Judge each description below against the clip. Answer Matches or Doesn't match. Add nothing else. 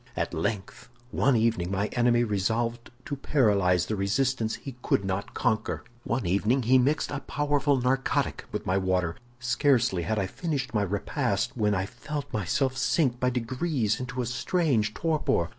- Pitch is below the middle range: Matches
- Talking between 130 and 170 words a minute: Matches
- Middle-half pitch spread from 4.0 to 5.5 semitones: Matches